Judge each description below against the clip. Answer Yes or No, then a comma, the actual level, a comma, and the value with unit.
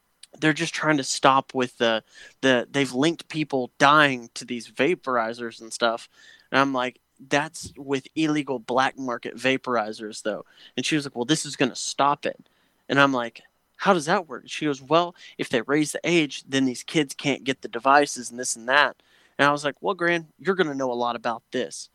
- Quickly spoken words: Yes, fast, 210 wpm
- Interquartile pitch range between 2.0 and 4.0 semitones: Yes, average, 3.3 semitones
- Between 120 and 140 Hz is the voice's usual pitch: Yes, low, 135 Hz